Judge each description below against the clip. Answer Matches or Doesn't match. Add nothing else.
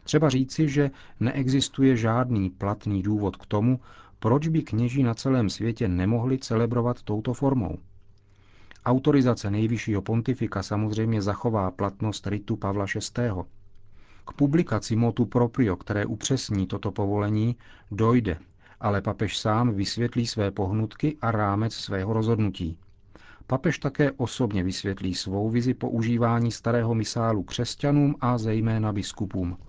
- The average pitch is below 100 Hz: Doesn't match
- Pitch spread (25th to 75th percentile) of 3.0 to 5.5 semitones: Matches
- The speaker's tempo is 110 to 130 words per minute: Matches